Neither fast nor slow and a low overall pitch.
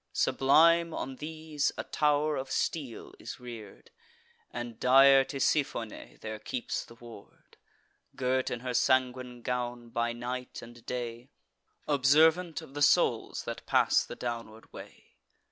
No: slow, 130 wpm; low, 125 Hz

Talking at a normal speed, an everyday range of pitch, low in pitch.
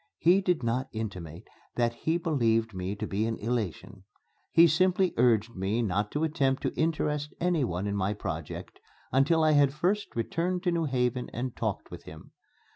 No: average, 175 wpm; wide, 7.0 semitones; low, 125 Hz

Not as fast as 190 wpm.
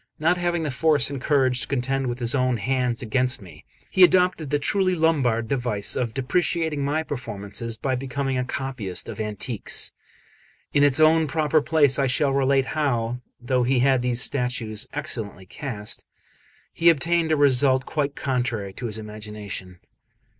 Yes: average, 160 wpm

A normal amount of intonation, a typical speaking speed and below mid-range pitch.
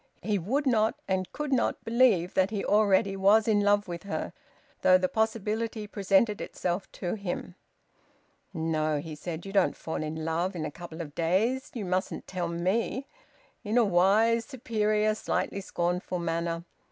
No: average, 4.0 semitones; average, 165 wpm; high, 195 Hz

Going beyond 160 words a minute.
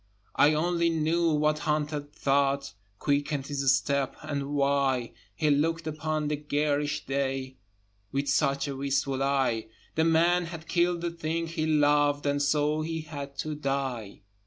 No: average, 150 wpm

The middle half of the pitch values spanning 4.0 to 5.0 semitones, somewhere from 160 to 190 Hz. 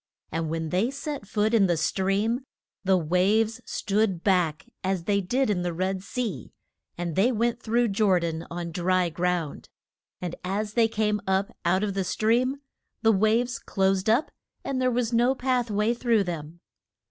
No: average, 4.4 semitones; high, 200 Hz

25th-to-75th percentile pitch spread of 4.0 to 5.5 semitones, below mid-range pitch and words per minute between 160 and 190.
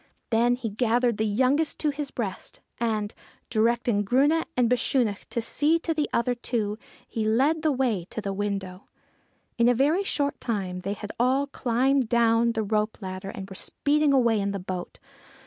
No: average, 4.4 semitones; high, 235 Hz; average, 180 wpm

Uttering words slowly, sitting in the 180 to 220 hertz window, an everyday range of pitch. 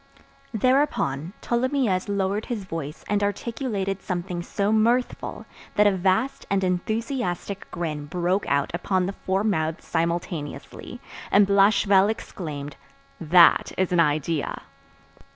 Yes: slow, 115 wpm; high, 190 Hz; average, 3.7 semitones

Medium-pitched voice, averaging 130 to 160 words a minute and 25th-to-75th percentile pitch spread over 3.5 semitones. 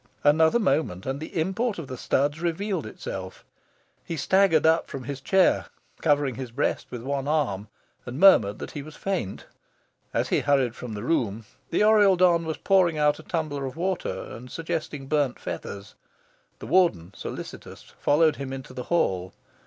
No: medium, 145 Hz; average, 170 wpm; average, 4.9 semitones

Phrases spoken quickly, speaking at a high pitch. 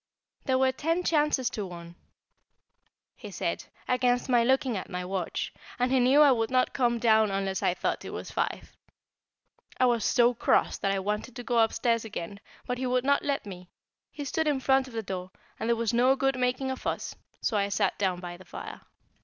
Yes: fast, 210 wpm; high, 240 Hz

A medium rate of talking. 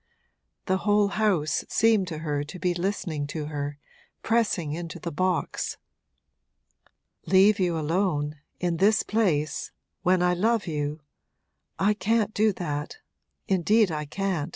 No: slow, 130 wpm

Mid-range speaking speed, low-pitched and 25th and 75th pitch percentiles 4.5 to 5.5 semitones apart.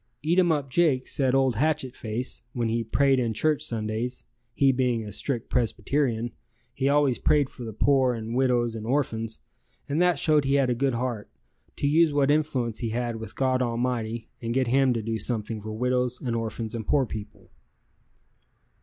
No: average, 180 wpm; low, 125 Hz; average, 3.2 semitones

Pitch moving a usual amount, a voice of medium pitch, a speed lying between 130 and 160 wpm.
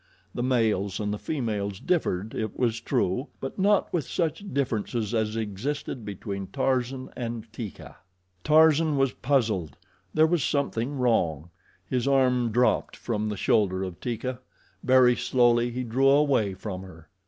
No: average, 4.4 semitones; low, 120 Hz; average, 145 wpm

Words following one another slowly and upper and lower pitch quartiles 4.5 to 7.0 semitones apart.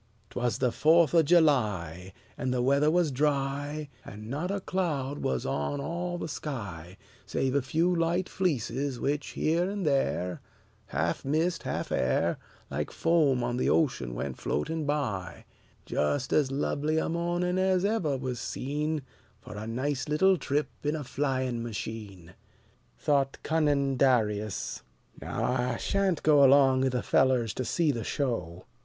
No: average, 155 wpm; average, 4.8 semitones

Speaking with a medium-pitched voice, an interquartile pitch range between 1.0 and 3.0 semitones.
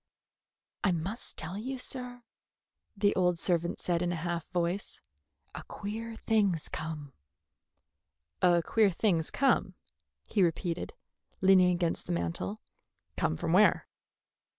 No: medium, 180 Hz; average, 3.7 semitones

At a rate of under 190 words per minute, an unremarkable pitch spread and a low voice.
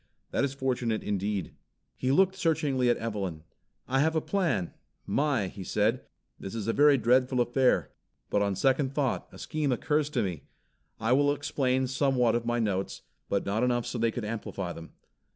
Yes: average, 180 wpm; average, 4.5 semitones; low, 125 Hz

